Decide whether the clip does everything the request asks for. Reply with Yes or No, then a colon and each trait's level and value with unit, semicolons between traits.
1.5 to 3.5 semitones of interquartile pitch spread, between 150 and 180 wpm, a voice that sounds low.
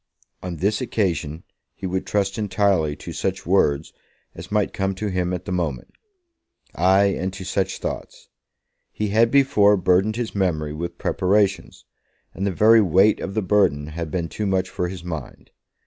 Yes: average, 2.9 semitones; average, 170 wpm; very low, 95 Hz